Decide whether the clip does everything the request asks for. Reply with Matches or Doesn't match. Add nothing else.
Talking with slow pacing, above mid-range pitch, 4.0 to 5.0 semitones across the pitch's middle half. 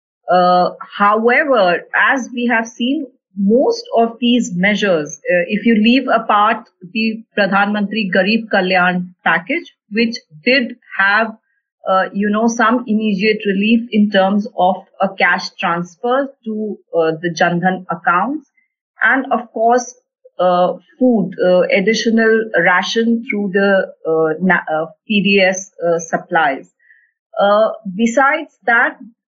Matches